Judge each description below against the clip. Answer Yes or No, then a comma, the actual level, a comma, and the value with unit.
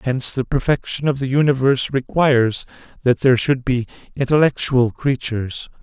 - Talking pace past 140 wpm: No, slow, 135 wpm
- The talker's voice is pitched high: No, low, 130 Hz